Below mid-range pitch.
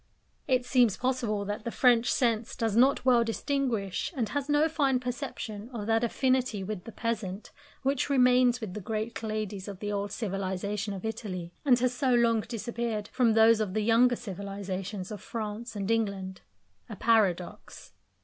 No: high, 225 Hz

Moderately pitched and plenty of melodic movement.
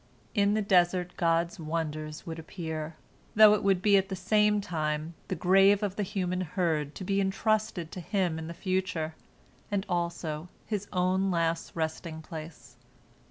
No: medium, 180 Hz; average, 3.3 semitones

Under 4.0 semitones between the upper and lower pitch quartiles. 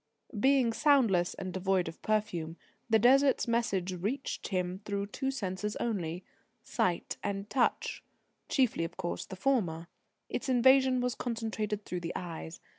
No: average, 5.3 semitones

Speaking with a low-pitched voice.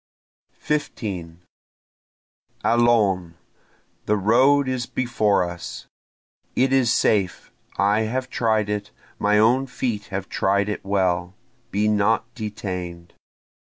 Yes: low, 105 Hz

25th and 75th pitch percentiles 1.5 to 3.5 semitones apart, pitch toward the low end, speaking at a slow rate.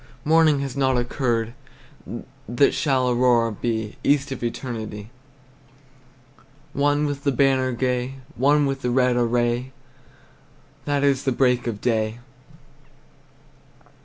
Yes: narrow, 2.6 semitones; low, 125 Hz; slow, 115 wpm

